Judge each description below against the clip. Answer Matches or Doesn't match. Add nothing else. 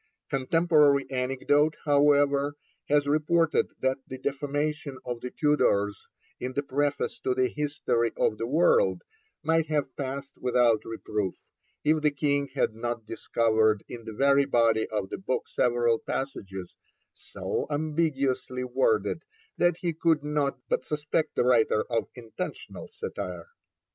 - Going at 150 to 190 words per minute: Doesn't match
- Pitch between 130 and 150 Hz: Matches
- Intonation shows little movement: Doesn't match